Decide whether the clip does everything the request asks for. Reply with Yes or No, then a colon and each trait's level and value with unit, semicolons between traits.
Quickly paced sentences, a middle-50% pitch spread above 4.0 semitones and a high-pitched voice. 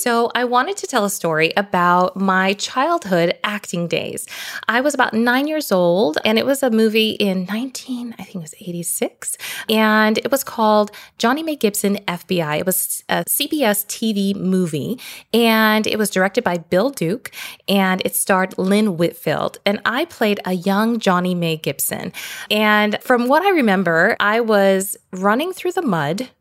No: average, 175 wpm; average, 4.5 semitones; high, 210 Hz